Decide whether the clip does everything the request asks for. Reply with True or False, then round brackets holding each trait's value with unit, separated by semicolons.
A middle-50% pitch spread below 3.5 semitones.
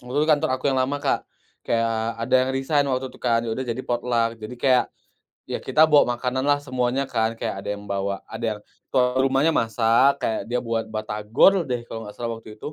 True (2.9 semitones)